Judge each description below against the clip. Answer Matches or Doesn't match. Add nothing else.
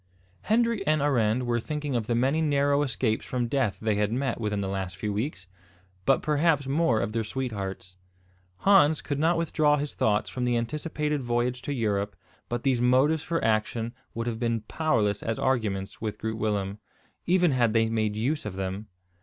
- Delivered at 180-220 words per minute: Matches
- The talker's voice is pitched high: Doesn't match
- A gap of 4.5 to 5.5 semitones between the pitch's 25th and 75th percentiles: Matches